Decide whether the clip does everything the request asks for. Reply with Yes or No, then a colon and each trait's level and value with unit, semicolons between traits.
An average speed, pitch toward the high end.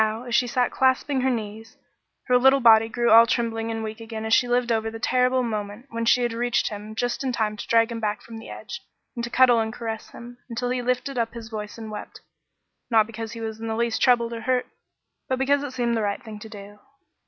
No: fast, 255 wpm; high, 230 Hz